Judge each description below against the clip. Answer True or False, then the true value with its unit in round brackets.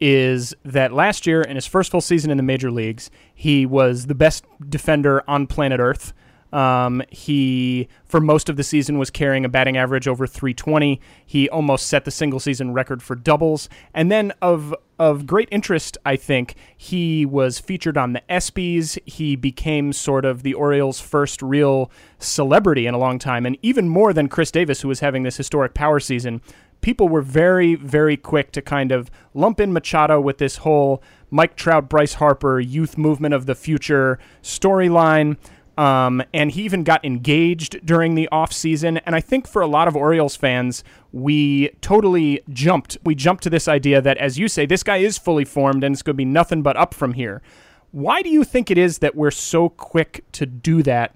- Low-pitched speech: False (145 Hz)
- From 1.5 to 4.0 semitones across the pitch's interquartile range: True (3.4 semitones)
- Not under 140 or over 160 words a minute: False (195 wpm)